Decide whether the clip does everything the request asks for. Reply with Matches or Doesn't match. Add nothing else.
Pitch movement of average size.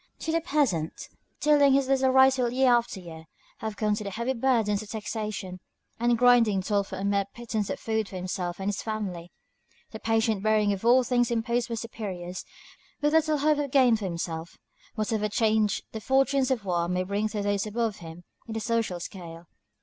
Matches